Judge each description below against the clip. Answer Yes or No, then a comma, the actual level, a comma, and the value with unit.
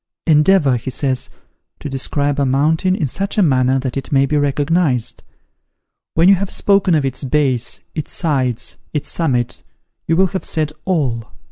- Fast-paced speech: No, average, 165 wpm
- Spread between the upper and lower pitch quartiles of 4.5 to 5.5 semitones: No, average, 4.0 semitones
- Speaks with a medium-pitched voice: Yes, medium, 145 Hz